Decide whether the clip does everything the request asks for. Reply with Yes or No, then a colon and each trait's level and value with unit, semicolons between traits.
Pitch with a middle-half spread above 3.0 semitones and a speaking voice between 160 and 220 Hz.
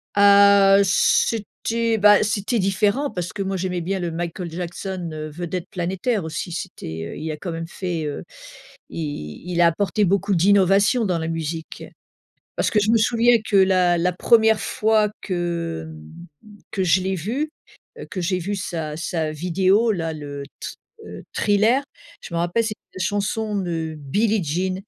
Yes: average, 3.5 semitones; medium, 185 Hz